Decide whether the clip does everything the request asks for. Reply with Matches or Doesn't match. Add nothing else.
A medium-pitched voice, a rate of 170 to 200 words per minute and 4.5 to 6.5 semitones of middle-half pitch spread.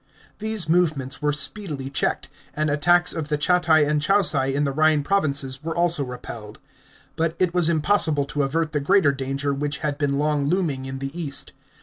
Doesn't match